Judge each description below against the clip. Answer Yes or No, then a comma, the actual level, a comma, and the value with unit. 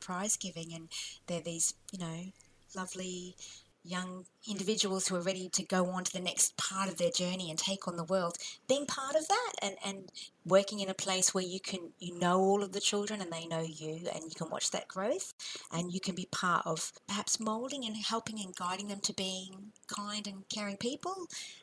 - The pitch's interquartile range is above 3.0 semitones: No, narrow, 2.4 semitones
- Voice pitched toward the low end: No, high, 190 Hz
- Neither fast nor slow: No, fast, 210 wpm